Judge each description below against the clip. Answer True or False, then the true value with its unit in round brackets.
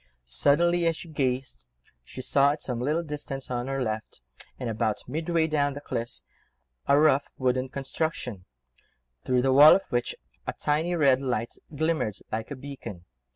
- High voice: False (135 Hz)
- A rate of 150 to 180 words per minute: True (160 wpm)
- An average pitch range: True (3.7 semitones)